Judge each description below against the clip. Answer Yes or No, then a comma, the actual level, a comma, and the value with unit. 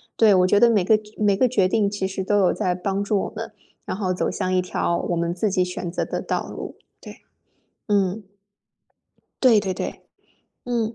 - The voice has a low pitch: No, high, 195 Hz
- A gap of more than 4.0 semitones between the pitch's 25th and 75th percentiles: No, narrow, 2.5 semitones